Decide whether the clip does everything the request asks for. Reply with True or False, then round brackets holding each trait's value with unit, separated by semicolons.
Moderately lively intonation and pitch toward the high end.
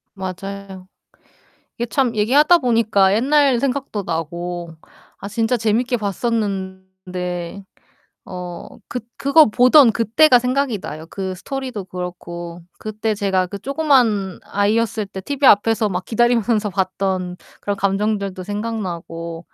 True (4.2 semitones; 205 Hz)